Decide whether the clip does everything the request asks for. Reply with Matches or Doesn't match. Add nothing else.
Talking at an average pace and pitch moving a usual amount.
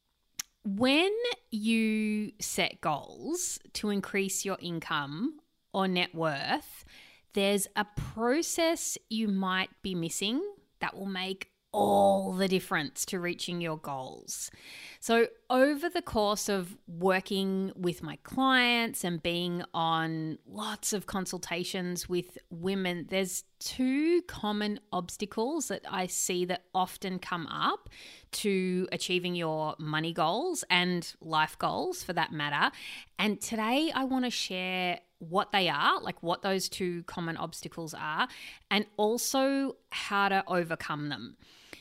Doesn't match